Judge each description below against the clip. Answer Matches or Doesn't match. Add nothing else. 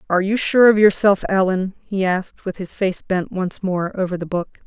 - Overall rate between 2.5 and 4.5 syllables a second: Doesn't match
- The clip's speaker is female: Matches